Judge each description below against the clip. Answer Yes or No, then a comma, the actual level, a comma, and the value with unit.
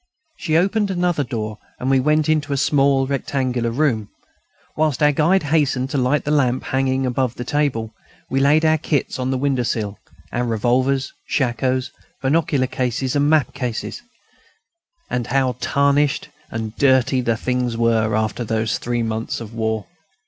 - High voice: No, low, 130 Hz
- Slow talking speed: No, average, 160 wpm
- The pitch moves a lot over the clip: No, average, 3.4 semitones